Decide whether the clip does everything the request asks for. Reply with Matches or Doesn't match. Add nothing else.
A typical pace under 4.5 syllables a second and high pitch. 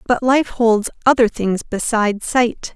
Matches